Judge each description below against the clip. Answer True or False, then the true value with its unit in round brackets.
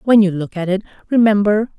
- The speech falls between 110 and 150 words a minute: False (200 wpm)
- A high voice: True (200 Hz)